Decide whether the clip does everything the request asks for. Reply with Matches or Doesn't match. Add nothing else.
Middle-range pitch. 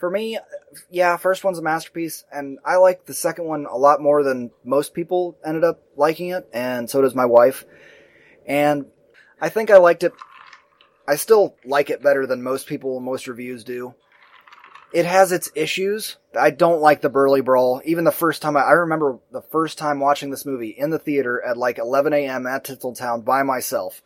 Matches